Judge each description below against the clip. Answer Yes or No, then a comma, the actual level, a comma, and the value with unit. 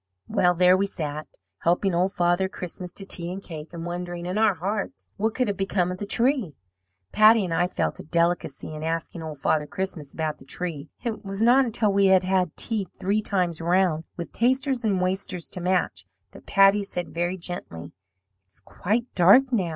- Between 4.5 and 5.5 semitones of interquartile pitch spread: No, average, 3.0 semitones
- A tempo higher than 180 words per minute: Yes, average, 195 wpm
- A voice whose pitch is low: No, medium, 185 Hz